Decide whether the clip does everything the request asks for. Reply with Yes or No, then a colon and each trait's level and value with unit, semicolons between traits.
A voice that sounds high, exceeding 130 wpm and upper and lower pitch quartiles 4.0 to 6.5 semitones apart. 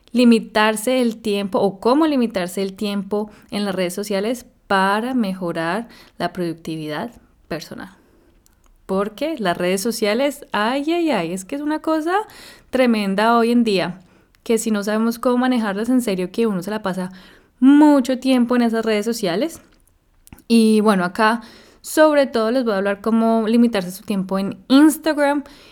Yes: high, 220 Hz; average, 155 wpm; average, 4.4 semitones